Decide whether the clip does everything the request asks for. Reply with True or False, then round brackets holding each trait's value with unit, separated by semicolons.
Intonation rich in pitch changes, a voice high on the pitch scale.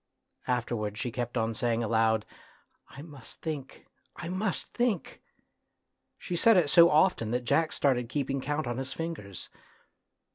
False (5.8 semitones; 135 Hz)